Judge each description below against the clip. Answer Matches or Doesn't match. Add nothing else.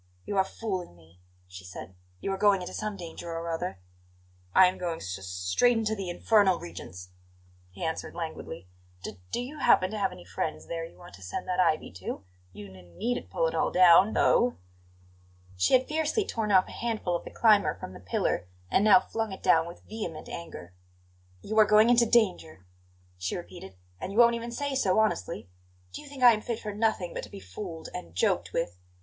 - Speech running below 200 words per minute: Doesn't match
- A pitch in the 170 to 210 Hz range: Matches